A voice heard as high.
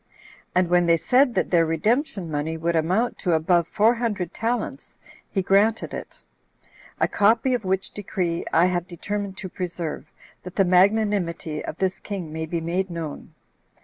No: medium, 180 Hz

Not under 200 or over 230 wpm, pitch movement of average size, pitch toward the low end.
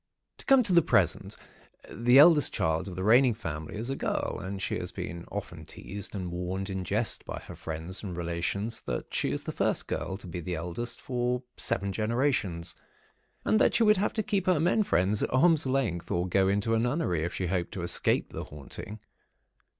No: fast, 205 wpm; wide, 6.8 semitones; low, 100 Hz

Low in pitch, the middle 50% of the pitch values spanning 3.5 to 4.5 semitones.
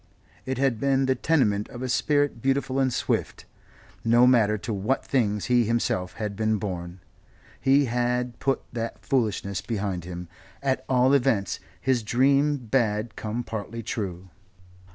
Yes: low, 120 Hz; average, 4.1 semitones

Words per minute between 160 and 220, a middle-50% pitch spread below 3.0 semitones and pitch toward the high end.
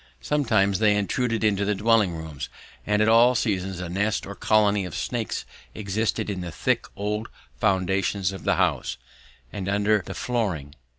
No: average, 165 wpm; narrow, 2.4 semitones; low, 100 Hz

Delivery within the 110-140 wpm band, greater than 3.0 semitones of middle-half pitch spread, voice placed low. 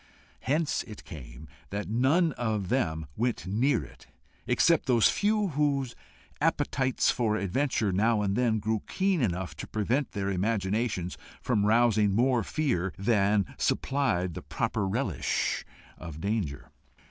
Yes: slow, 135 wpm; average, 5.0 semitones; low, 110 Hz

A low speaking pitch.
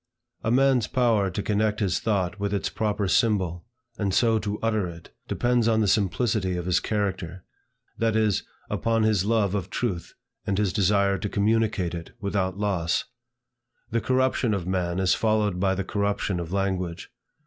Yes: low, 100 Hz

